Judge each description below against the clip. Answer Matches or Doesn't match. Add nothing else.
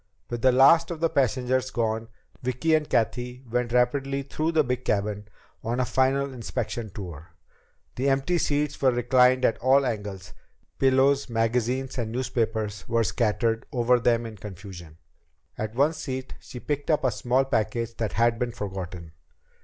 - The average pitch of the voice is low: Matches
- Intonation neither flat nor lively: Matches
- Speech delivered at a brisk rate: Doesn't match